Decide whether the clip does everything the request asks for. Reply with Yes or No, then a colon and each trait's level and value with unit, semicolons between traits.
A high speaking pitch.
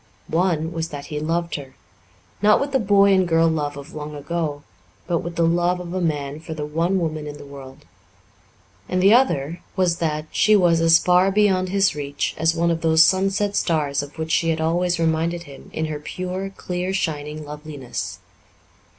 No: medium, 165 Hz